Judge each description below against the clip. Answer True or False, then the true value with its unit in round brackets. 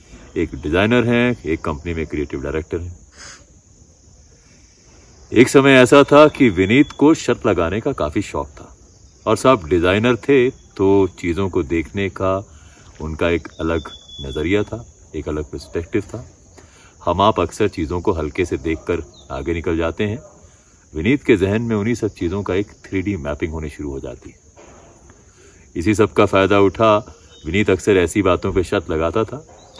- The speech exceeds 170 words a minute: False (160 wpm)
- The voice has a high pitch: False (95 Hz)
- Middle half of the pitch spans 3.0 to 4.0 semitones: False (4.7 semitones)